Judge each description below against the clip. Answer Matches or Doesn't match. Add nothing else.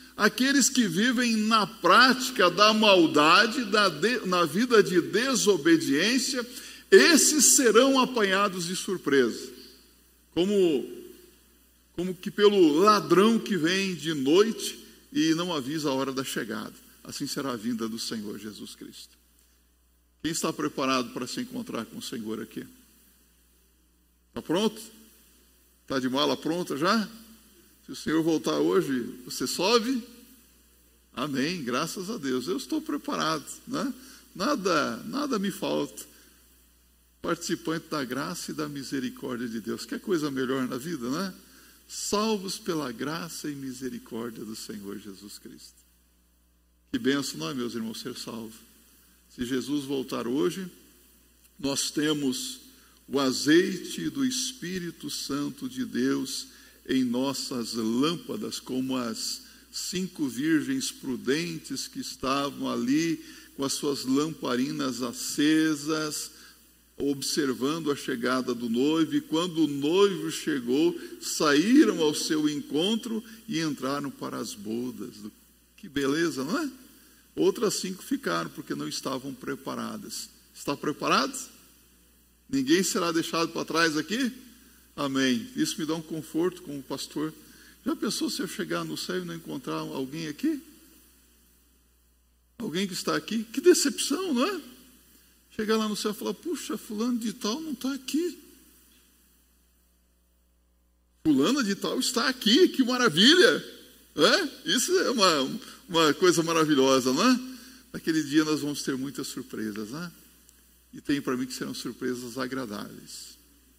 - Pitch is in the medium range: Matches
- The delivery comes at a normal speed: Matches